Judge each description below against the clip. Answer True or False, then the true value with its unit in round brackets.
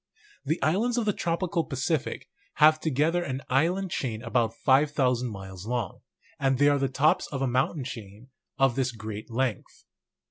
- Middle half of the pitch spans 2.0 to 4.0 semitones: False (4.6 semitones)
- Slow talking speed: False (165 wpm)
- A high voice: False (135 Hz)